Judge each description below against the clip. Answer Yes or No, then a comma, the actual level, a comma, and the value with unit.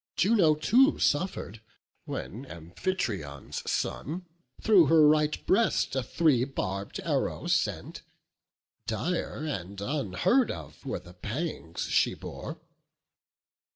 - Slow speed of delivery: Yes, slow, 105 wpm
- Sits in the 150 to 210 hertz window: No, medium, 140 Hz